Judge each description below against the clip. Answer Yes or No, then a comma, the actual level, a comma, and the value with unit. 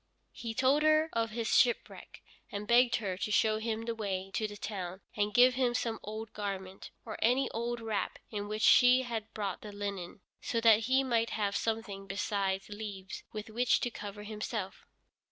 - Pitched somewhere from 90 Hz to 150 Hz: No, high, 215 Hz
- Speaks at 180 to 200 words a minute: Yes, average, 185 wpm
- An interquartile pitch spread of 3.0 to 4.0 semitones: No, narrow, 2.5 semitones